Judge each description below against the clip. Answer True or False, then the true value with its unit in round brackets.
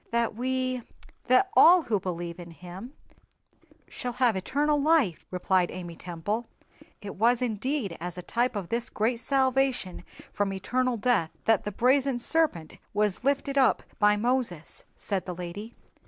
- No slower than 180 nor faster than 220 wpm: False (145 wpm)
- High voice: True (230 Hz)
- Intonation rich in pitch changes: True (5.7 semitones)